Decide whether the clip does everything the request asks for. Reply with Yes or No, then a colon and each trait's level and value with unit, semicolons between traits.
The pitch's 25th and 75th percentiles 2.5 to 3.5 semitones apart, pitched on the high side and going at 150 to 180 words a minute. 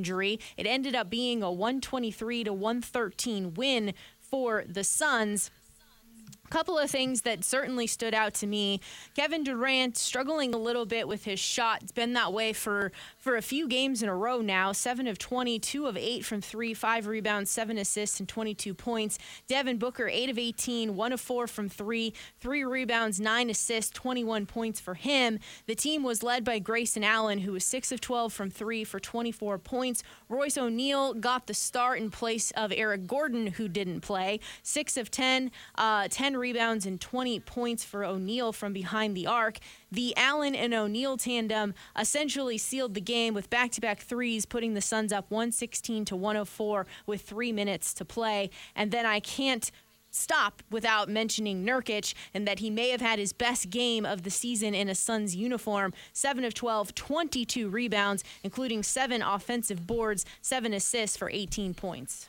Yes: average, 3.0 semitones; high, 225 Hz; average, 175 wpm